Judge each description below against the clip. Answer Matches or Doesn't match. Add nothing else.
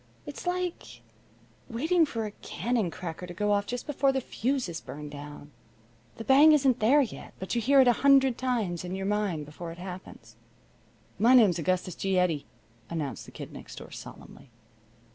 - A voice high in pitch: Matches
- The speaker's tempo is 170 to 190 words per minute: Matches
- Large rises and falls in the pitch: Matches